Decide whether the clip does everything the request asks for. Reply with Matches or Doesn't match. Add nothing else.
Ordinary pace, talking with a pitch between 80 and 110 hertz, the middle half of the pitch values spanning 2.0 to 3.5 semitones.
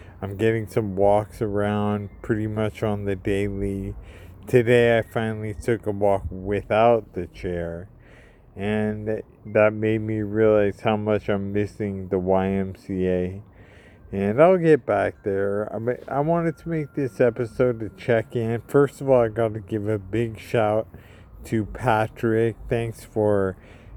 Matches